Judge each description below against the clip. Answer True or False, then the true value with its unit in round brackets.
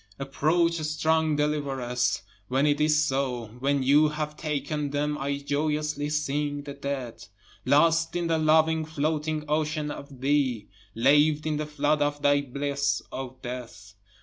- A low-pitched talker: False (145 Hz)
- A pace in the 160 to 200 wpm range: False (145 wpm)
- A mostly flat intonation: True (1.7 semitones)